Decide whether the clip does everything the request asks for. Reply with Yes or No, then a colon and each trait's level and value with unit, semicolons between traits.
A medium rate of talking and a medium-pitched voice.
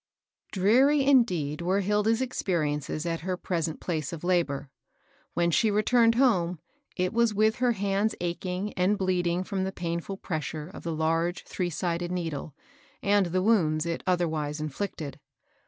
Yes: average, 155 wpm; medium, 180 Hz